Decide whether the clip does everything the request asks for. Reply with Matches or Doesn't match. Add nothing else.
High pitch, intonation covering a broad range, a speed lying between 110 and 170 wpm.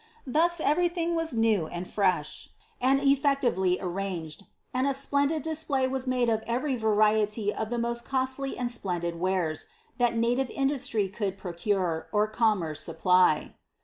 Matches